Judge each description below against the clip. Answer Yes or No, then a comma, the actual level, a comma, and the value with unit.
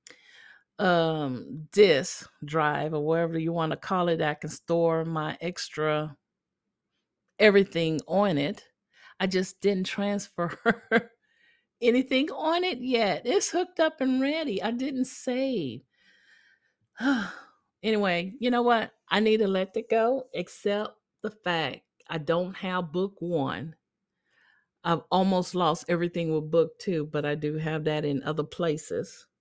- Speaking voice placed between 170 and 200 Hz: Yes, medium, 185 Hz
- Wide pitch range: Yes, wide, 6.0 semitones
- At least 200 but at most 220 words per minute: No, slow, 135 wpm